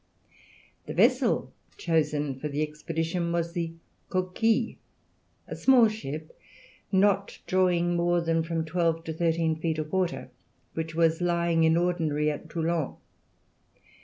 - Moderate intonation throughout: No, narrow, 1.7 semitones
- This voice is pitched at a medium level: Yes, medium, 165 Hz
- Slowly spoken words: Yes, slow, 130 wpm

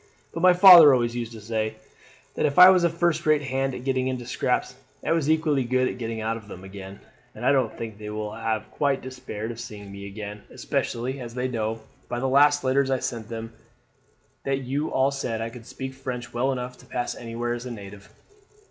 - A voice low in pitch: Yes, low, 125 Hz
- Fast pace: Yes, fast, 220 wpm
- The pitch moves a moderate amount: Yes, average, 3.3 semitones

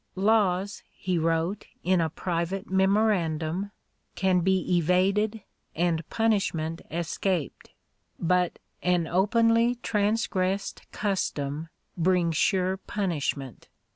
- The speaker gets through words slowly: Yes, slow, 90 wpm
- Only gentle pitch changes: No, average, 3.1 semitones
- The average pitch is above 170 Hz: Yes, medium, 185 Hz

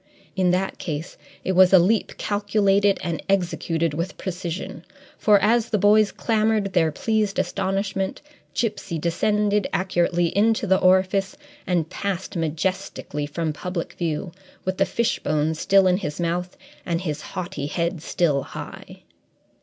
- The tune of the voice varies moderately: Yes, average, 3.0 semitones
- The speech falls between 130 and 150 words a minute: Yes, average, 140 wpm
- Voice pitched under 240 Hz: Yes, medium, 185 Hz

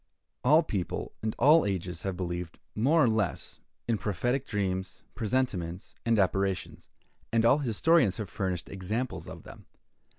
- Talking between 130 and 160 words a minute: Yes, average, 140 wpm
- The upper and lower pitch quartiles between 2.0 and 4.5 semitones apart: No, average, 5.1 semitones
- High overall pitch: No, low, 105 Hz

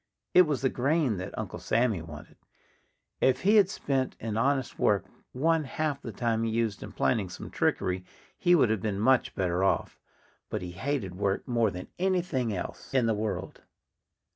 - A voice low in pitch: Yes, low, 115 Hz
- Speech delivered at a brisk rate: No, average, 180 wpm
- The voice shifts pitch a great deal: Yes, wide, 5.7 semitones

